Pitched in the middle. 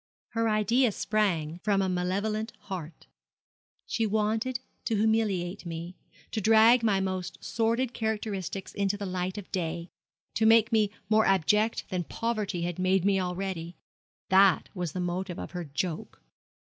No: high, 195 Hz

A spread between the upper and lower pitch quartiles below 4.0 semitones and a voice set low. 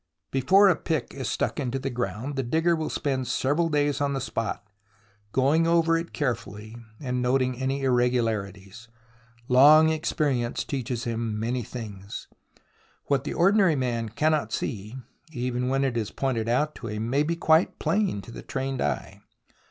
No: average, 4.3 semitones; low, 130 Hz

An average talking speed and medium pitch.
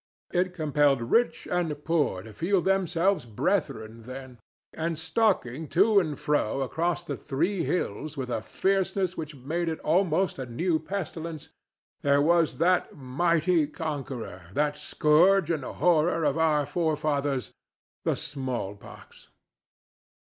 No: slow, 125 wpm; medium, 155 Hz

